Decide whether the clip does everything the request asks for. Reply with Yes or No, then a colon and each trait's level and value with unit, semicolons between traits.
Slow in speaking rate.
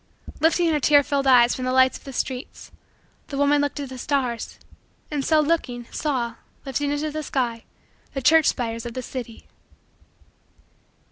No: average, 165 wpm